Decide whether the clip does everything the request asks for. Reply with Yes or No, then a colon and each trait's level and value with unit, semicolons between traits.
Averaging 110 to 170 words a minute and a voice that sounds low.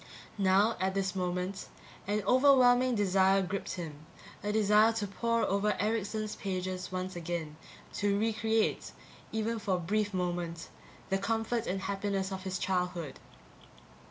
No: average, 140 wpm; high, 195 Hz